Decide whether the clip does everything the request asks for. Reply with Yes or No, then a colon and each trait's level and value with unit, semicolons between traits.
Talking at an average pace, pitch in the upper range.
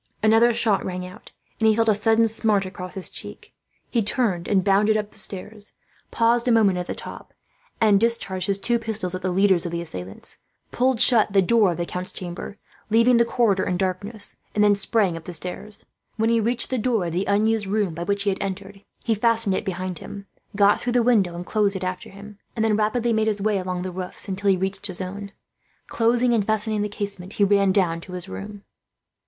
No: fast, 225 wpm; high, 205 Hz